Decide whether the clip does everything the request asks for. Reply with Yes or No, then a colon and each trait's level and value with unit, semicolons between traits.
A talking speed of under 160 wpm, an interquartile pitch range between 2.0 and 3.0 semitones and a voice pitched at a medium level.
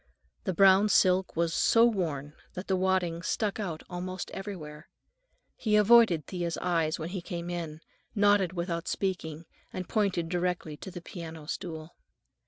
Yes: average, 150 wpm; average, 2.7 semitones; medium, 180 Hz